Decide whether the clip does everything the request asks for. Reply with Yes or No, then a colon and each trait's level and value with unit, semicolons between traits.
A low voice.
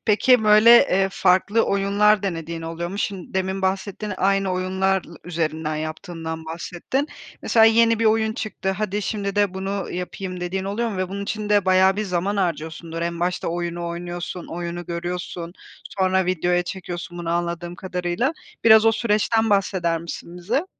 No: medium, 185 Hz